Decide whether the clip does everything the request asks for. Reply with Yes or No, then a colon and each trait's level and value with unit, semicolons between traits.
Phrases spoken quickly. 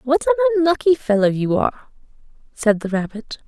No: average, 155 wpm